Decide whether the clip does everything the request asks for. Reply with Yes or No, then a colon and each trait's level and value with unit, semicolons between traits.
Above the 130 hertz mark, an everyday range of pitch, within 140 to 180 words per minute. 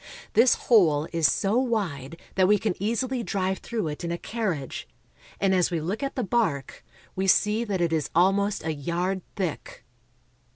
Yes: high, 190 Hz; average, 4.5 semitones; average, 175 wpm